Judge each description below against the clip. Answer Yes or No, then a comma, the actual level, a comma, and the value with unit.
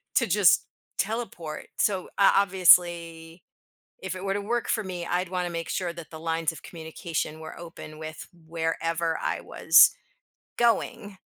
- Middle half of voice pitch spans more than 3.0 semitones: No, narrow, 2.6 semitones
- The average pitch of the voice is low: No, medium, 170 Hz